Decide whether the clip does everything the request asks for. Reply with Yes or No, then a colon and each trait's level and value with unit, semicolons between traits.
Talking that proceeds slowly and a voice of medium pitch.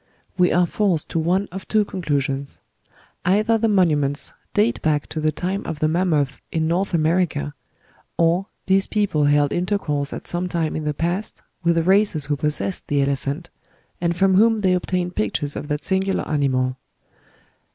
No: average, 165 wpm; medium, 170 Hz